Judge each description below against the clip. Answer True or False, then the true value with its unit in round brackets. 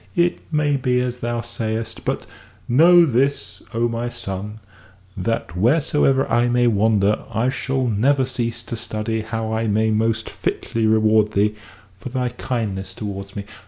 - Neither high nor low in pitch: False (115 Hz)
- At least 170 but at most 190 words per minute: False (155 wpm)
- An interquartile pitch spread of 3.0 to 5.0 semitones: False (2.5 semitones)